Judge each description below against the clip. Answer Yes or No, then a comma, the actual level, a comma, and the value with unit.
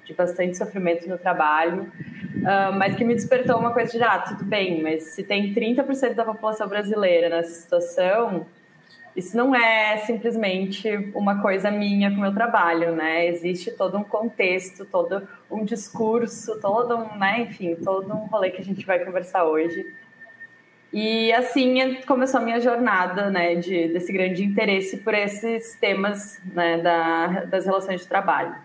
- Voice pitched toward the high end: Yes, high, 200 Hz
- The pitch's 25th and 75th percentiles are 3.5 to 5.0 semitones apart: Yes, average, 4.0 semitones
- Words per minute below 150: No, average, 155 wpm